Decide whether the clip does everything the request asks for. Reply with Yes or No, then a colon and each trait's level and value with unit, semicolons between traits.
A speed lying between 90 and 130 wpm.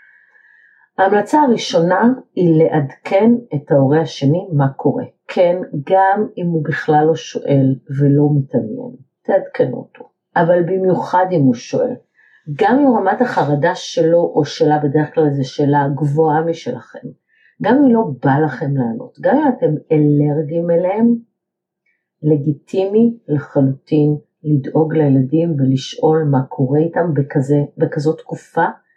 Yes: average, 125 wpm